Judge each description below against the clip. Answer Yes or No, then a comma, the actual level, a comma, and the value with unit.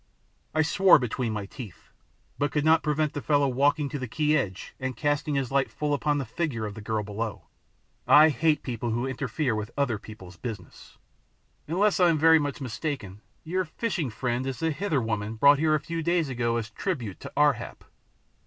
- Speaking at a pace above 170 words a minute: Yes, average, 200 wpm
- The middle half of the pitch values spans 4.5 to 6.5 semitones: Yes, average, 5.2 semitones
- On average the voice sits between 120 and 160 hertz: Yes, medium, 140 Hz